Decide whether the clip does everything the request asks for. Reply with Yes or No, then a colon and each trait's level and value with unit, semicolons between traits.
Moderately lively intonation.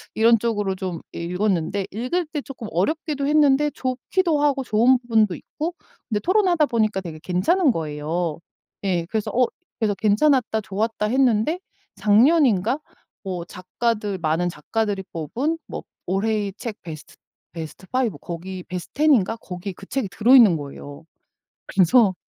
No: wide, 6.1 semitones